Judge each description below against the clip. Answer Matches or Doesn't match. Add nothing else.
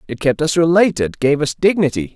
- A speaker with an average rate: Matches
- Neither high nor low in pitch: Matches